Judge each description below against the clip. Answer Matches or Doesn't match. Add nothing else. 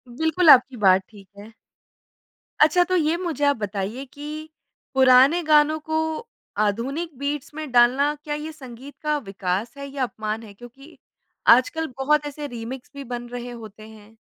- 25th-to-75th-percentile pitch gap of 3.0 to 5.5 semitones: Matches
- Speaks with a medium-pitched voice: Doesn't match